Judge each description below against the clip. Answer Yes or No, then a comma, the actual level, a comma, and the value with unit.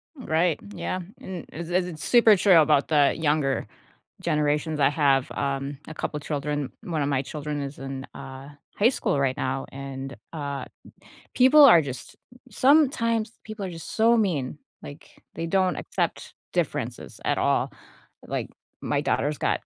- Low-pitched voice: No, medium, 150 Hz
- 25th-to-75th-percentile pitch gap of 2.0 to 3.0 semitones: No, average, 5.0 semitones